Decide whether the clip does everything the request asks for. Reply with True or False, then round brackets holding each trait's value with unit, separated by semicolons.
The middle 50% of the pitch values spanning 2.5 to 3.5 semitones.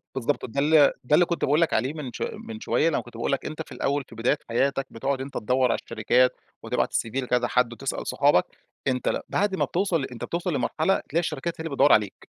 False (4.3 semitones)